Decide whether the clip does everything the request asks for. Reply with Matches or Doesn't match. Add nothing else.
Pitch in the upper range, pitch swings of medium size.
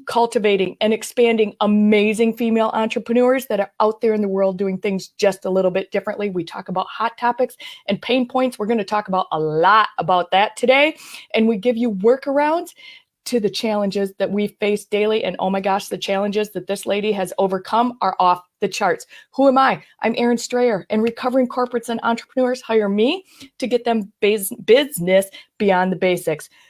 Matches